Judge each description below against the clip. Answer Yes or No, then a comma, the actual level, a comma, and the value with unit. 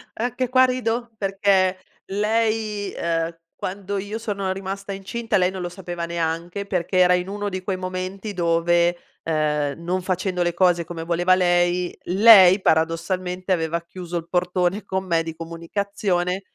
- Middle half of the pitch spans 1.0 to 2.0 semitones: No, narrow, 2.5 semitones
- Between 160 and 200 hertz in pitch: Yes, medium, 185 Hz